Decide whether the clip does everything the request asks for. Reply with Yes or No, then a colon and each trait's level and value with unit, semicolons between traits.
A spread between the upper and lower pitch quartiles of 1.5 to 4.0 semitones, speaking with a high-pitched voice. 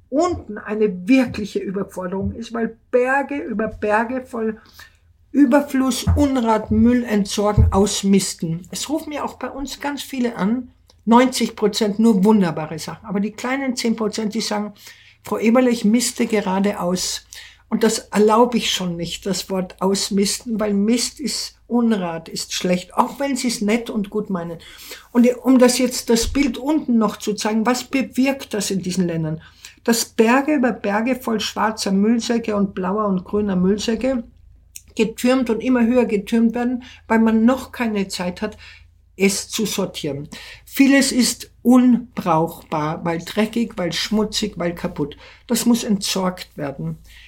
Yes: average, 3.7 semitones; high, 220 Hz